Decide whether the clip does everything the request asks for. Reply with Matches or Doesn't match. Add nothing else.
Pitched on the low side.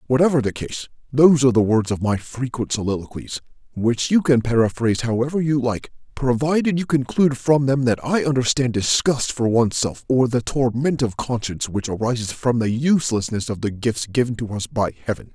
Matches